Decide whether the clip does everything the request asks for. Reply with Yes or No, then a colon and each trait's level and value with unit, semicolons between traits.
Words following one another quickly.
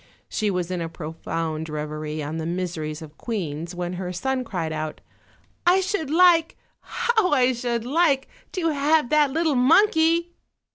No: average, 160 wpm